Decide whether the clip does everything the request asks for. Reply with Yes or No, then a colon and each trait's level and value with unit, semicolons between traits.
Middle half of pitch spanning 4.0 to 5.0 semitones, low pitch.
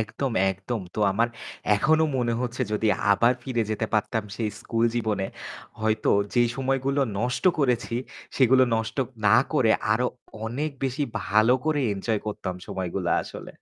No: average, 3.2 semitones; low, 115 Hz